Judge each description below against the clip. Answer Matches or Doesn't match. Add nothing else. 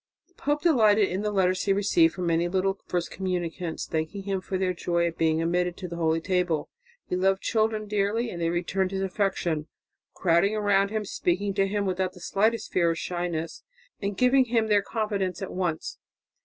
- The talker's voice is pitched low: Doesn't match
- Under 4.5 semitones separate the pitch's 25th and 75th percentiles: Matches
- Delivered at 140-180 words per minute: Doesn't match